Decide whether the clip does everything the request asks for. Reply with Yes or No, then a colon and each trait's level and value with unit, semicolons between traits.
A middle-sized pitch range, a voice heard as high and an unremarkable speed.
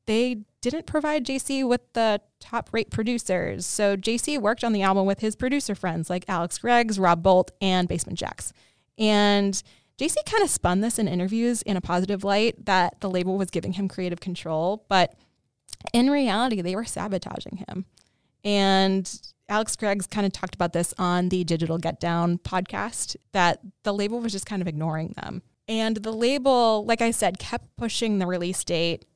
Yes: average, 3.9 semitones; high, 200 Hz; average, 180 wpm